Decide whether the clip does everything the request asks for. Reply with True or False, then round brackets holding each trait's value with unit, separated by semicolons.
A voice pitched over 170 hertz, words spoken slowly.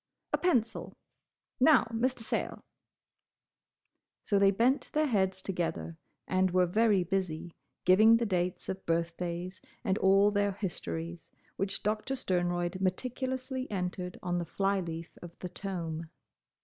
True (190 Hz; 130 wpm)